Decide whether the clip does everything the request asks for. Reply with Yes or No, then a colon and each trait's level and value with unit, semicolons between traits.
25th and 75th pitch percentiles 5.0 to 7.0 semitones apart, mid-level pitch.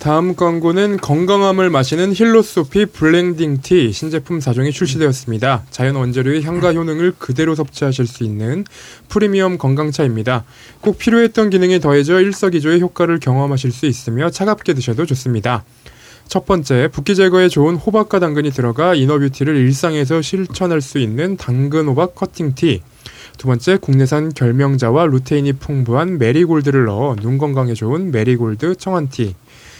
Yes: wide, 5.5 semitones; medium, 150 Hz